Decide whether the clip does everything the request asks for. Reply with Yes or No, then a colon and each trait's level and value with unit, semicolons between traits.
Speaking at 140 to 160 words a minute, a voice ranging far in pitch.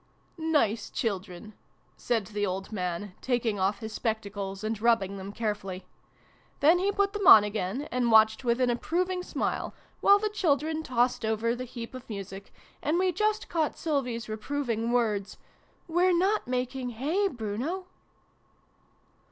Yes: average, 155 wpm; wide, 7.0 semitones